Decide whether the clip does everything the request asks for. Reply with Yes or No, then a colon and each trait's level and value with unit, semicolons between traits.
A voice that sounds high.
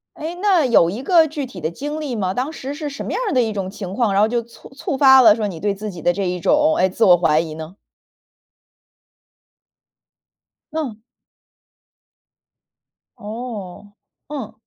Yes: high, 220 Hz